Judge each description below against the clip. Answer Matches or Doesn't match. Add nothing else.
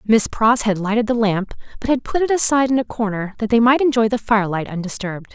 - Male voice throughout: Doesn't match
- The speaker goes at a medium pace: Doesn't match